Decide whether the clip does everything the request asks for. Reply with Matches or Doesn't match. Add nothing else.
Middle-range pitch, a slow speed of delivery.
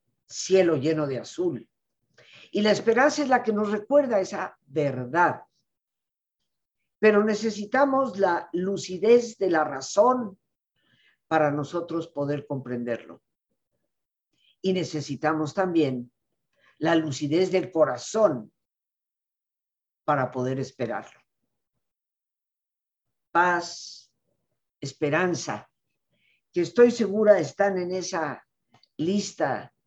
Matches